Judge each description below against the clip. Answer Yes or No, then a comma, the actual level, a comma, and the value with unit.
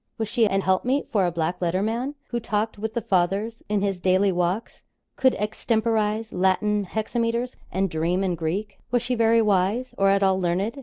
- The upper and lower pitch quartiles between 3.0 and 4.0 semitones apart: Yes, average, 3.3 semitones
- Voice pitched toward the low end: No, high, 205 Hz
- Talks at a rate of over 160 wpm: Yes, average, 190 wpm